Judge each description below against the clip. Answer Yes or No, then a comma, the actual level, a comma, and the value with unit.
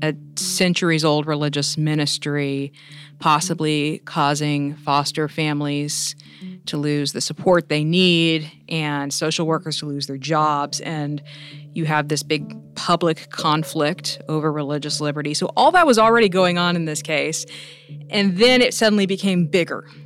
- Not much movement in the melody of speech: Yes, narrow, 2.2 semitones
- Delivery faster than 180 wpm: No, average, 145 wpm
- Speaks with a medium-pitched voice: Yes, medium, 150 Hz